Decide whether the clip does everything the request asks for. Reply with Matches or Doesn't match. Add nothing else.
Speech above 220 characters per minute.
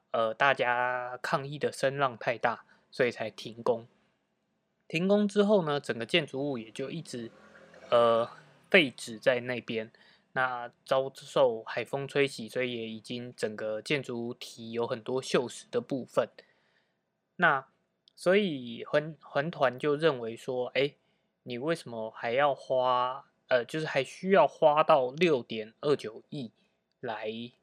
Doesn't match